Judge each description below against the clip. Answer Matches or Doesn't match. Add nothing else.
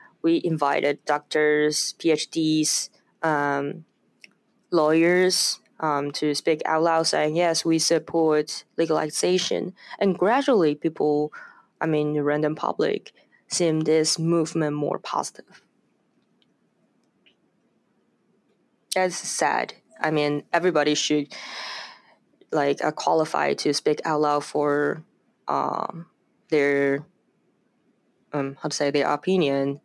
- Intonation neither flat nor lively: Doesn't match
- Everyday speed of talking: Doesn't match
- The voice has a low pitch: Doesn't match